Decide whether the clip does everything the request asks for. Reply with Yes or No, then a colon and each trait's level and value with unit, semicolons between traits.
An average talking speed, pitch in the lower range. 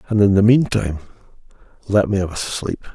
Yes: average, 185 wpm; low, 100 Hz